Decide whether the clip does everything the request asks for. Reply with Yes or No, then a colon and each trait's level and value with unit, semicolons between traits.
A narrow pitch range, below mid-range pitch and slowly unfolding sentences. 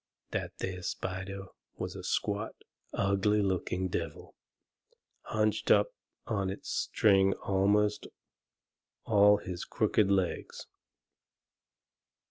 Yes: narrow, 1.7 semitones; low, 100 Hz; slow, 95 wpm